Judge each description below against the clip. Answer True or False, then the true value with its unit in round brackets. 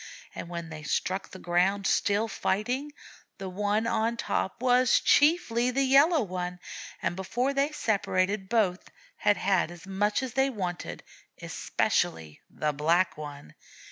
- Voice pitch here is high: True (200 Hz)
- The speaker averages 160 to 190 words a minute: False (140 wpm)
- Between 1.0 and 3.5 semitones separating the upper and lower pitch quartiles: False (5.5 semitones)